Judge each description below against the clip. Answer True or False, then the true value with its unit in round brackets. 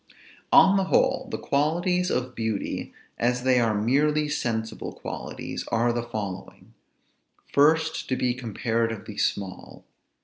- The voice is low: True (120 Hz)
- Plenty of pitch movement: False (4.9 semitones)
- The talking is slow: True (125 wpm)